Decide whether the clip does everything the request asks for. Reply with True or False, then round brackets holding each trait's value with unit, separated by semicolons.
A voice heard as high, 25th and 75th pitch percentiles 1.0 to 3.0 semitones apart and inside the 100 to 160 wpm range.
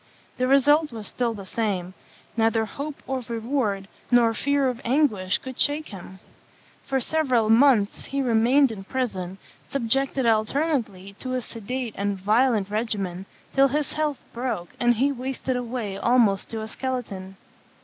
False (235 Hz; 4.3 semitones; 150 wpm)